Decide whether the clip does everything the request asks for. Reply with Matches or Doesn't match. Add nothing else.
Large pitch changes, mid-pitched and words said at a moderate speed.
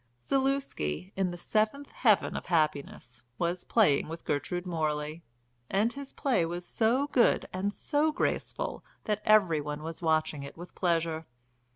Matches